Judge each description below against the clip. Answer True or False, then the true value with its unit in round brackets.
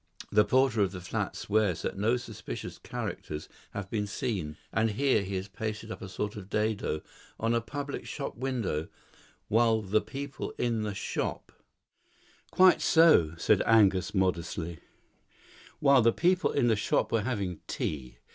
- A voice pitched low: True (110 Hz)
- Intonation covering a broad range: False (4.1 semitones)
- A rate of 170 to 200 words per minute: False (160 wpm)